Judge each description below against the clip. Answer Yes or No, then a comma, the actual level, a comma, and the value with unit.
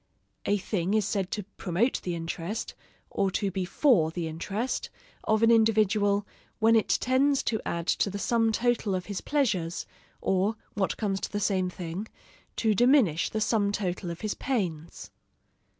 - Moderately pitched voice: No, high, 205 Hz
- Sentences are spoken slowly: No, average, 165 wpm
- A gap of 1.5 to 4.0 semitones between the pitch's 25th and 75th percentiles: Yes, average, 3.5 semitones